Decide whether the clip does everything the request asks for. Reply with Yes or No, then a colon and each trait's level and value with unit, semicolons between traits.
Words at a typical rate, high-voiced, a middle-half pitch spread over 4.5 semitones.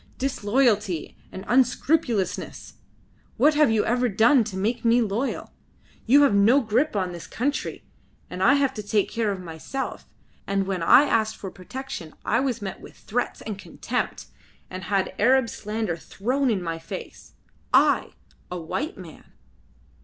Yes: average, 155 wpm; high, 220 Hz; average, 5.1 semitones